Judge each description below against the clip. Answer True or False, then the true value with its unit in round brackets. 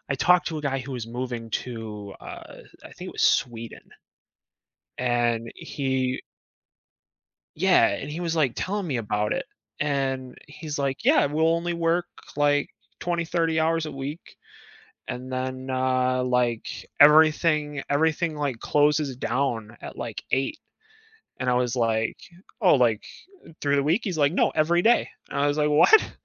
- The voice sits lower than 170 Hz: True (140 Hz)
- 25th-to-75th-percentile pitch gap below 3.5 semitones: False (3.9 semitones)